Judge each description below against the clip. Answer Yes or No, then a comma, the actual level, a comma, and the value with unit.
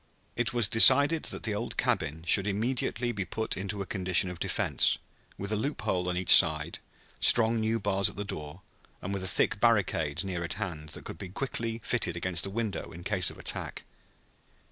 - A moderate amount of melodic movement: Yes, average, 4.0 semitones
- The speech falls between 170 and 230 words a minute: Yes, average, 195 wpm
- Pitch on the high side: No, low, 100 Hz